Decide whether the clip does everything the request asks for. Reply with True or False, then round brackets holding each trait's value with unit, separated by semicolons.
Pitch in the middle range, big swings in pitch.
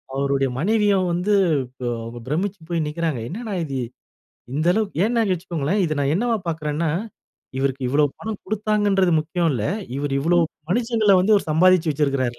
True (170 Hz; 5.9 semitones)